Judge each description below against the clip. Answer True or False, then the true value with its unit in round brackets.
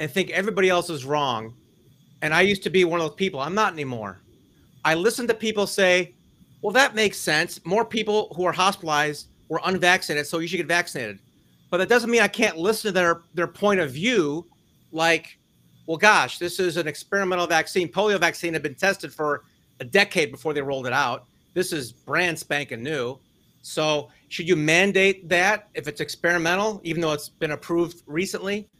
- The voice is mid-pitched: True (175 Hz)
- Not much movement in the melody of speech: False (3.9 semitones)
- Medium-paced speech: True (190 wpm)